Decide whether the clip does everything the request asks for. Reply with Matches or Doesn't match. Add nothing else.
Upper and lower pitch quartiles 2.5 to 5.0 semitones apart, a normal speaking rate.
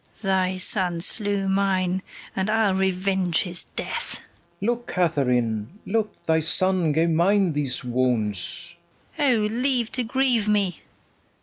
Doesn't match